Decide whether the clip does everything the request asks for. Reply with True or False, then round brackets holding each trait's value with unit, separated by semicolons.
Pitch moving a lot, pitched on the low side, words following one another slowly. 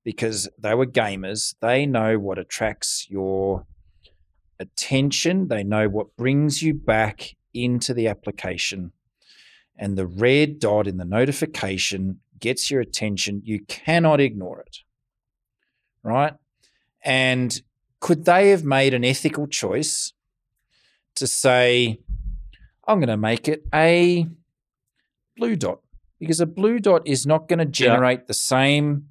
True (5.9 semitones; 125 Hz; 130 wpm)